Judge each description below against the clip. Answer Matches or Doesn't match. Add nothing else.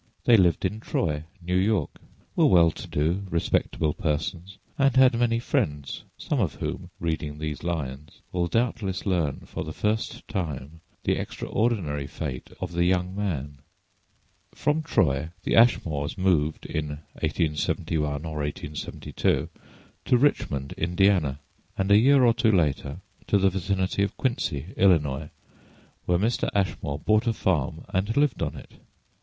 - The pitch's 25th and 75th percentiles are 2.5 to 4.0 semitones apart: Doesn't match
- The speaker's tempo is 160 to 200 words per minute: Doesn't match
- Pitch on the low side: Matches